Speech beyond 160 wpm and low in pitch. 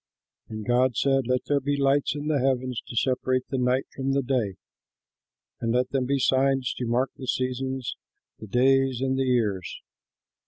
Yes: average, 170 wpm; low, 130 Hz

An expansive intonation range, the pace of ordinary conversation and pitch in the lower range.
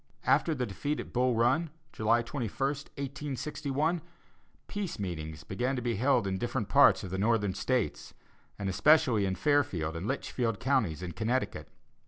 Yes: wide, 6.0 semitones; average, 155 wpm; low, 120 Hz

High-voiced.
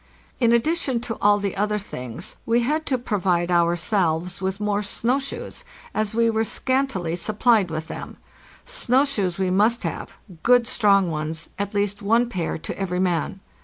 Yes: high, 205 Hz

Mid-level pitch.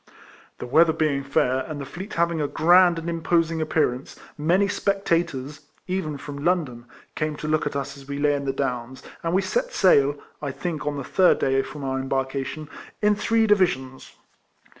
Yes: medium, 150 Hz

